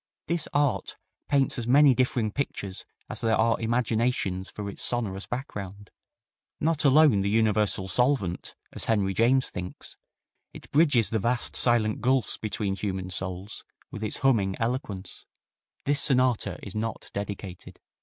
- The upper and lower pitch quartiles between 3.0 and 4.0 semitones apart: No, average, 4.4 semitones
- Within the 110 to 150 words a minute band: Yes, average, 140 wpm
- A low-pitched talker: Yes, low, 110 Hz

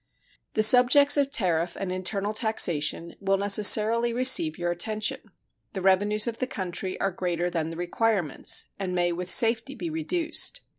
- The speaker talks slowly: No, average, 155 wpm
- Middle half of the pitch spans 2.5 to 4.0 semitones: No, average, 4.9 semitones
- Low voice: No, high, 200 Hz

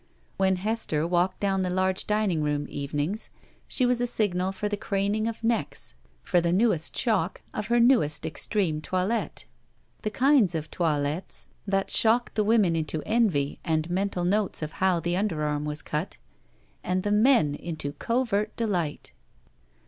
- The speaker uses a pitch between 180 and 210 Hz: Yes, high, 190 Hz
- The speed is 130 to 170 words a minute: Yes, average, 155 wpm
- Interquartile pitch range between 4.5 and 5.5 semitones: Yes, average, 5.0 semitones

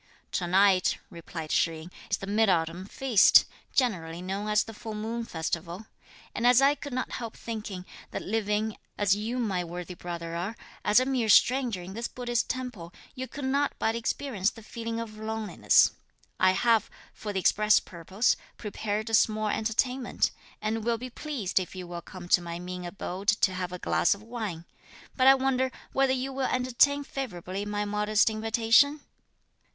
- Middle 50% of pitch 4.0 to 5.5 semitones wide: Yes, average, 4.6 semitones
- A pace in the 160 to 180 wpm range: Yes, average, 175 wpm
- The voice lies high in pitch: Yes, high, 215 Hz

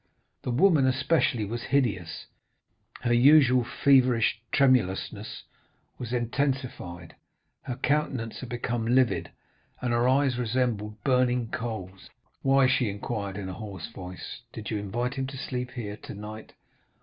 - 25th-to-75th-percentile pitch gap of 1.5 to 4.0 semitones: Yes, average, 3.4 semitones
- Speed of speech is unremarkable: No, slow, 130 wpm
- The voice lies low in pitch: Yes, low, 120 Hz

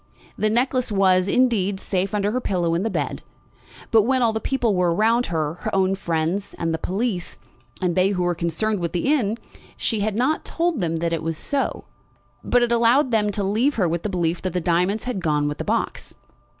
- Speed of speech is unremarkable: No, fast, 215 wpm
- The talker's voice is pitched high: Yes, high, 195 Hz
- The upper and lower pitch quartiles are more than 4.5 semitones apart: Yes, average, 4.9 semitones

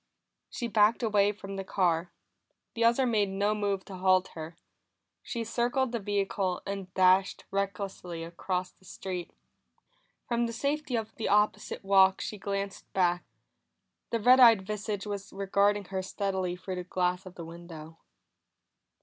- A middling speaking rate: Yes, average, 150 wpm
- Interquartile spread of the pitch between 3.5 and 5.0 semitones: No, narrow, 2.5 semitones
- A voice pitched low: No, high, 195 Hz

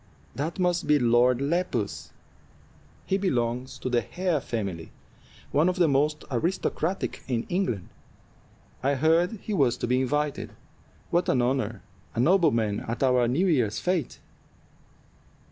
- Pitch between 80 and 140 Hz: Yes, low, 135 Hz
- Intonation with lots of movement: Yes, wide, 6.1 semitones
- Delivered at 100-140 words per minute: Yes, slow, 135 wpm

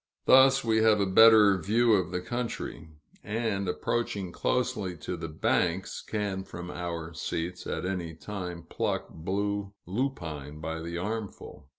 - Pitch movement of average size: Yes, average, 4.4 semitones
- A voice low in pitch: Yes, very low, 95 Hz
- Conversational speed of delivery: Yes, average, 145 wpm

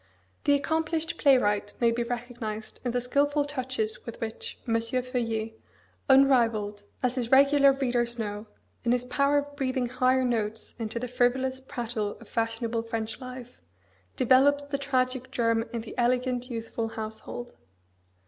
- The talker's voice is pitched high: Yes, high, 245 Hz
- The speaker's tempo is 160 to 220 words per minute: No, average, 145 wpm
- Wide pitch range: No, narrow, 2.5 semitones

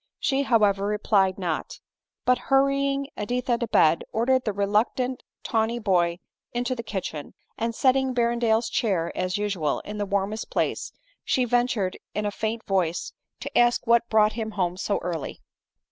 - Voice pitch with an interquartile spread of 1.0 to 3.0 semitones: No, average, 3.8 semitones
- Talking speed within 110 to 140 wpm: No, average, 155 wpm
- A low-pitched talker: No, high, 220 Hz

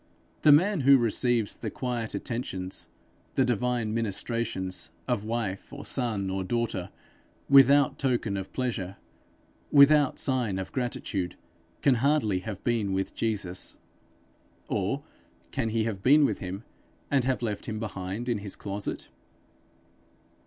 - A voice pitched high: No, low, 115 Hz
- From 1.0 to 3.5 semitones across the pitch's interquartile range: No, average, 4.5 semitones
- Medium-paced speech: No, slow, 130 wpm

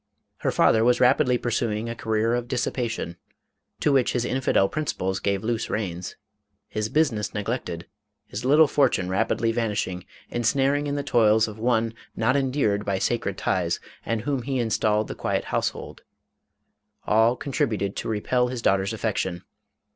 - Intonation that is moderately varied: Yes, average, 3.3 semitones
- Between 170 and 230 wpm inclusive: No, average, 160 wpm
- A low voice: Yes, low, 115 Hz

